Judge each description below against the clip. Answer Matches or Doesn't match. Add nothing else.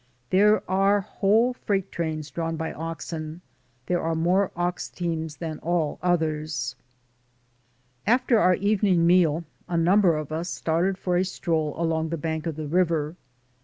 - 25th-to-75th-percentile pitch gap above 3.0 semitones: Doesn't match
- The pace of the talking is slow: Doesn't match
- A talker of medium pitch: Matches